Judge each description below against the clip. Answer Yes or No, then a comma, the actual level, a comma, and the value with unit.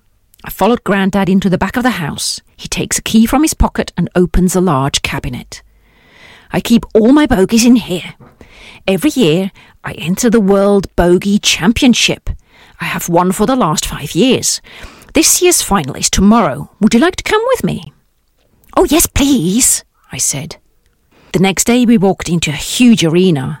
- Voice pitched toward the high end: Yes, high, 195 Hz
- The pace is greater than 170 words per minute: Yes, average, 180 wpm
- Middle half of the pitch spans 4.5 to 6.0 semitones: Yes, wide, 5.4 semitones